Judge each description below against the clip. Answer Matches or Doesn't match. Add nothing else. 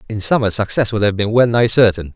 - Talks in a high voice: Doesn't match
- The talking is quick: Matches